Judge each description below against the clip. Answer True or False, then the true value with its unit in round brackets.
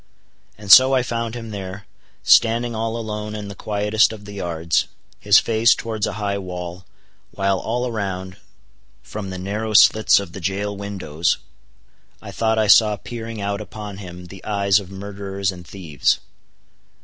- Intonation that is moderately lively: False (2.3 semitones)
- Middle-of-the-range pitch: False (100 Hz)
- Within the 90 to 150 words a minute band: False (160 wpm)